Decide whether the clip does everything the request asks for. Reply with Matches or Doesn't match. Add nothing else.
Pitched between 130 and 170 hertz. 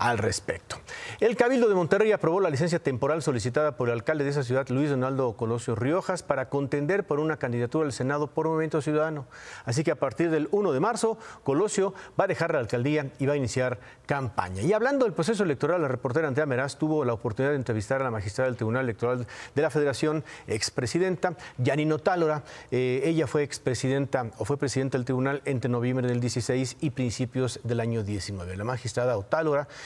Matches